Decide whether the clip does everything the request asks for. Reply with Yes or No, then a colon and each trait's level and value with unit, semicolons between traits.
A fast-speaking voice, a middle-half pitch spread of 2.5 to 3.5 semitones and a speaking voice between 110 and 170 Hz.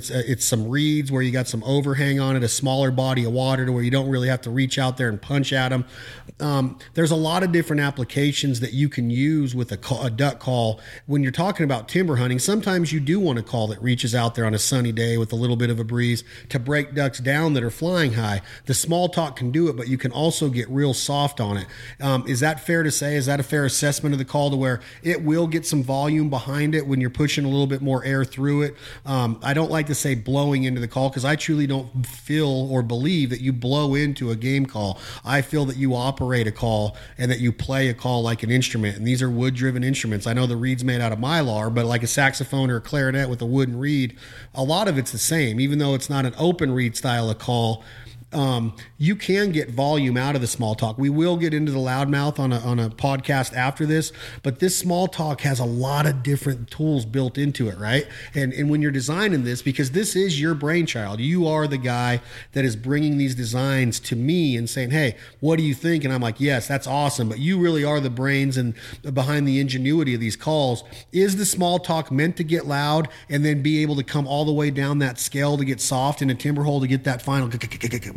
Yes: fast, 250 wpm; average, 3.1 semitones; low, 135 Hz